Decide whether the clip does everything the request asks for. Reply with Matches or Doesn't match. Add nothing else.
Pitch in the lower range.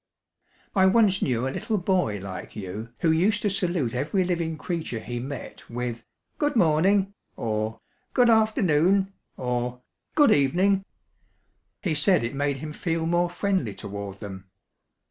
Doesn't match